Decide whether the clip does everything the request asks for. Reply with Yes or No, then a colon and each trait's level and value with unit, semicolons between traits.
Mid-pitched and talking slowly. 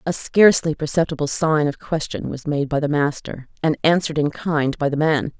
No: medium, 150 Hz; average, 200 wpm